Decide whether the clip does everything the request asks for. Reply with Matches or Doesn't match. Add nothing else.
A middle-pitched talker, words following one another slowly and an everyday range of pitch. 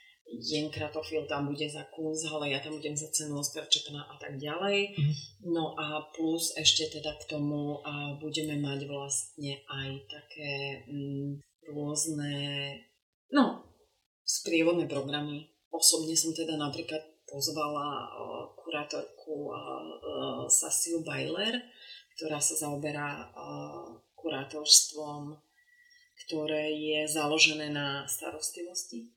Doesn't match